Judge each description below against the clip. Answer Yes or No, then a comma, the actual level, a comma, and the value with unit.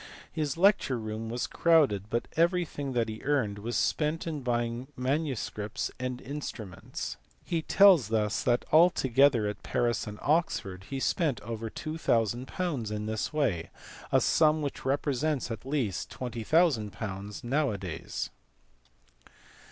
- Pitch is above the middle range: No, low, 125 Hz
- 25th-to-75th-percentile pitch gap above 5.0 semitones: Yes, wide, 5.6 semitones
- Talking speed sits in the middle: No, slow, 130 wpm